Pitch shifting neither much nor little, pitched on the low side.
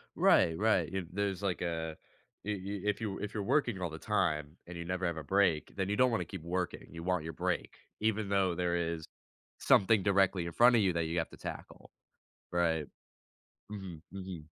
Yes: average, 3.1 semitones; very low, 90 Hz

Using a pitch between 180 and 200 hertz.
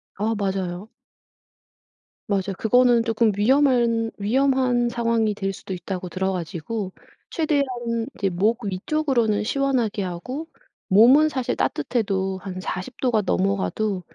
No: high, 215 Hz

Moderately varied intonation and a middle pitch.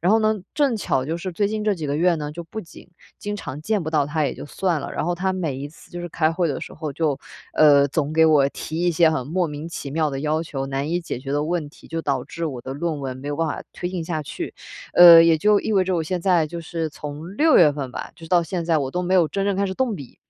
Yes: average, 3.3 semitones; medium, 165 Hz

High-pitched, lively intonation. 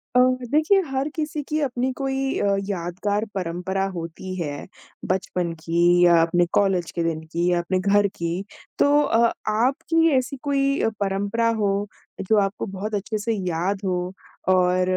Yes: high, 195 Hz; wide, 5.8 semitones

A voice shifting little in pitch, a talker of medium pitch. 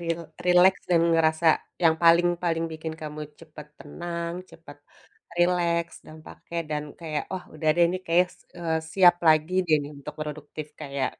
Yes: narrow, 2.0 semitones; medium, 165 Hz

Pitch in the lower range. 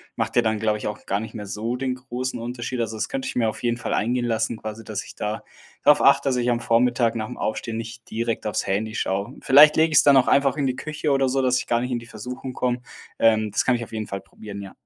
Yes: low, 120 Hz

